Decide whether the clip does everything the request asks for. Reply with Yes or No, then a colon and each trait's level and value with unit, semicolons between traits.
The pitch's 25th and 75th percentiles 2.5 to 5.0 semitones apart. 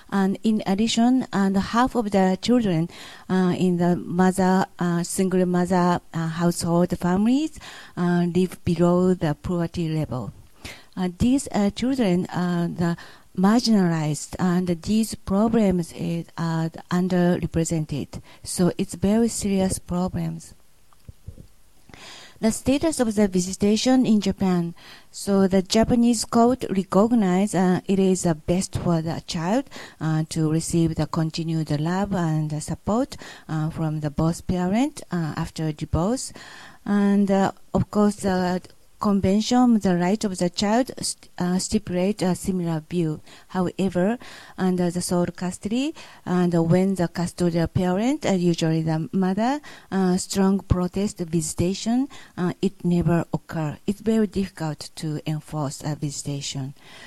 Yes: average, 3.2 semitones